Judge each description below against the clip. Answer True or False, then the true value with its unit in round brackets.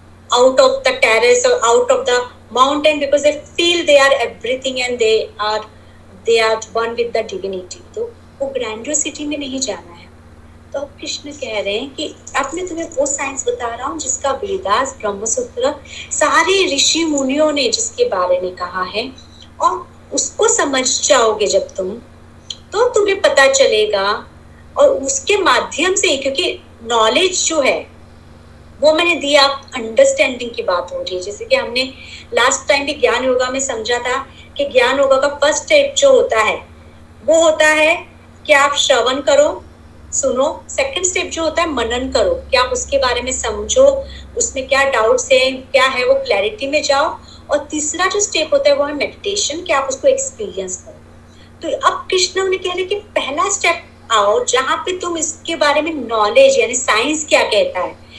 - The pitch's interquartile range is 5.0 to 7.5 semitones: True (5.3 semitones)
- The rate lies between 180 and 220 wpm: False (155 wpm)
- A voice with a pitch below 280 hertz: False (290 Hz)